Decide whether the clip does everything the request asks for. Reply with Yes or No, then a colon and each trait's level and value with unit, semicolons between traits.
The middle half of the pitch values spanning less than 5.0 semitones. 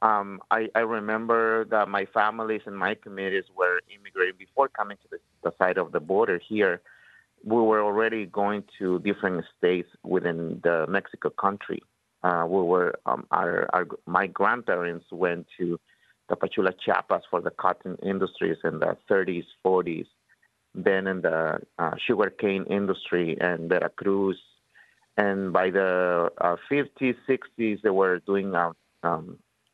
Yes: average, 3.1 semitones